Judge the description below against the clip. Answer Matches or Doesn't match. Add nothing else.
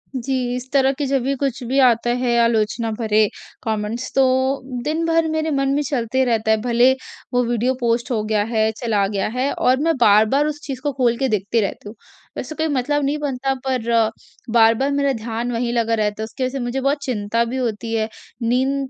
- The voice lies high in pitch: Matches